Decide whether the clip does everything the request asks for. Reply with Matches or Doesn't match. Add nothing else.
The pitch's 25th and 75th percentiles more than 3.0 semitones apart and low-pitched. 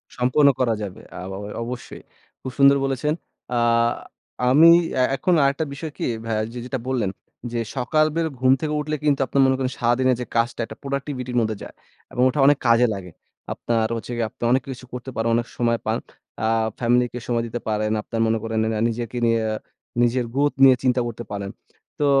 Doesn't match